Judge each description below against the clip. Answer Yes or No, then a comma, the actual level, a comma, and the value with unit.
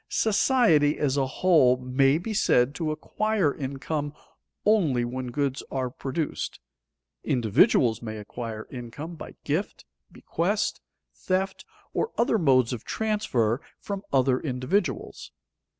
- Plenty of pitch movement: Yes, wide, 6.3 semitones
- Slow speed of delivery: Yes, slow, 120 wpm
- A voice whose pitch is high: No, medium, 140 Hz